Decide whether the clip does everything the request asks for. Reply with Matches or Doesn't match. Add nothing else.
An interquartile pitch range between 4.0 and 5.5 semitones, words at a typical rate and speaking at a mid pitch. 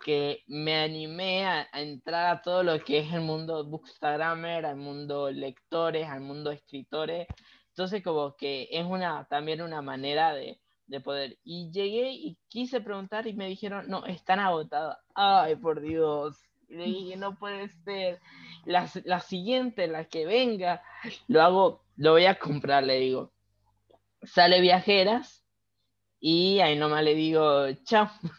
Matches